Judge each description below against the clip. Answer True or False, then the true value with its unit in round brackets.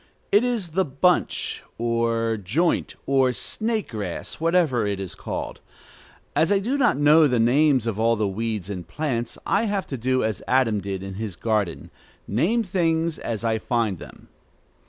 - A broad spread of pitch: True (7.3 semitones)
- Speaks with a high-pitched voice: False (120 Hz)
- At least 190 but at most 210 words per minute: False (170 wpm)